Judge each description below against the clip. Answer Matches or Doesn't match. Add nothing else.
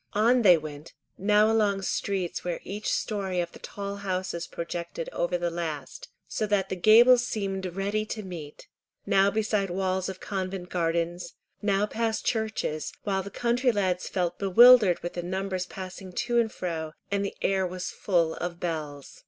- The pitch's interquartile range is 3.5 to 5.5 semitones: Doesn't match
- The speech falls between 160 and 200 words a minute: Matches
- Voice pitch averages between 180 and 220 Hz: Matches